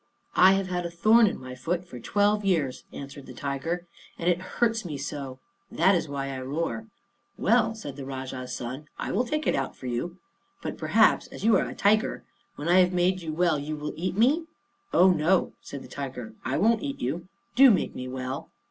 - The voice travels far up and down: Yes, wide, 6.1 semitones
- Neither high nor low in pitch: Yes, medium, 170 Hz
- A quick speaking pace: Yes, fast, 210 wpm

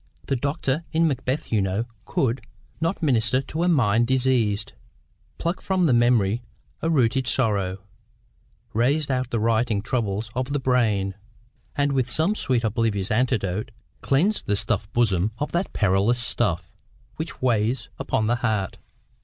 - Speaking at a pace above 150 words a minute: No, average, 145 wpm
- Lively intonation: No, average, 4.2 semitones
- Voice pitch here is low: Yes, low, 120 Hz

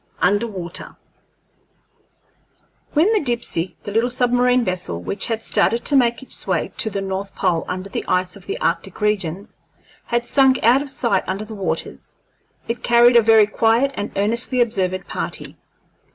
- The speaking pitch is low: No, high, 225 Hz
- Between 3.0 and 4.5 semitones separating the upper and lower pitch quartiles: Yes, average, 4.0 semitones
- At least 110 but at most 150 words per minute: No, average, 165 wpm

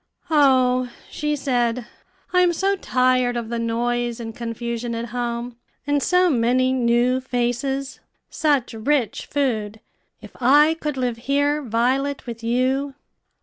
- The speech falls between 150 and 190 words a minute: No, slow, 135 wpm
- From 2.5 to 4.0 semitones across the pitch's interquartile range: Yes, average, 2.9 semitones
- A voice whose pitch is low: No, very high, 250 Hz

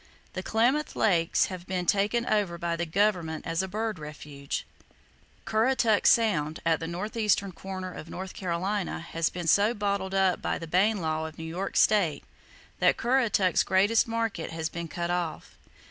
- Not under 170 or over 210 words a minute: Yes, average, 175 wpm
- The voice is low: No, medium, 185 Hz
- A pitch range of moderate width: Yes, average, 4.0 semitones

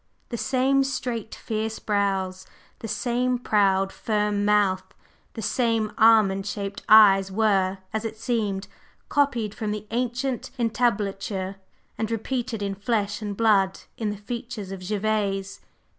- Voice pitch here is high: Yes, high, 210 Hz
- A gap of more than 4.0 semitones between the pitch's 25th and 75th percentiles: No, average, 2.7 semitones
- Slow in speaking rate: Yes, slow, 130 wpm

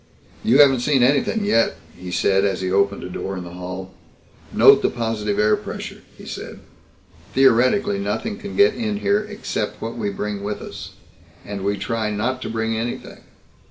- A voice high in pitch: No, low, 115 Hz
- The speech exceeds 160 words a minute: Yes, average, 180 wpm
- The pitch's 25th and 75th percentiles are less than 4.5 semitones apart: No, wide, 5.6 semitones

